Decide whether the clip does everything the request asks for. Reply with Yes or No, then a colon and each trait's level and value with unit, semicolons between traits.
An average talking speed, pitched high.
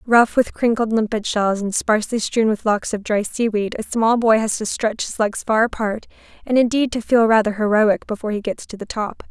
No: fast, 225 wpm; high, 220 Hz